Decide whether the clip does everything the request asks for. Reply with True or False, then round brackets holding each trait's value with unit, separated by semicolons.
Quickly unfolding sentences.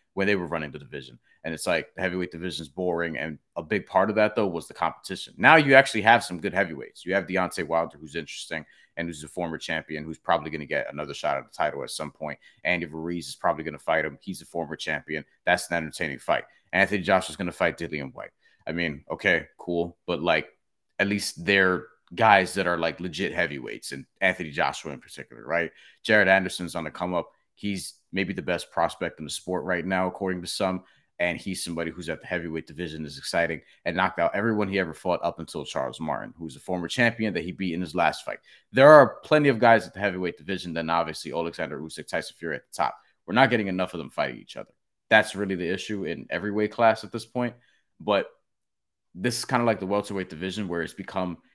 True (235 wpm)